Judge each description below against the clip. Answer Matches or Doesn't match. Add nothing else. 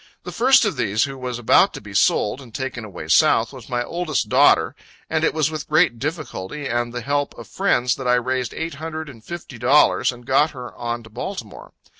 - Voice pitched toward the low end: Matches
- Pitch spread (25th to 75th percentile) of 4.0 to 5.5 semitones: Matches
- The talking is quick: Matches